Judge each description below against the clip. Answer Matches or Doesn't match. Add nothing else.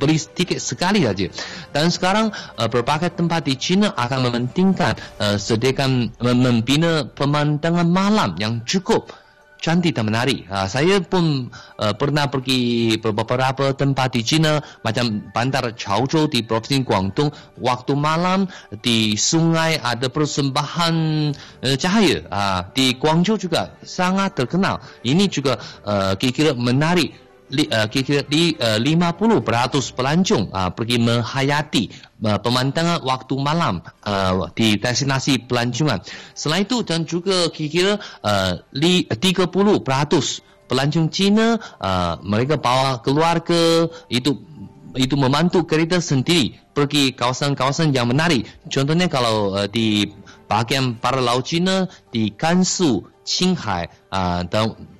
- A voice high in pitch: Doesn't match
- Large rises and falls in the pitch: Matches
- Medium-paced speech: Matches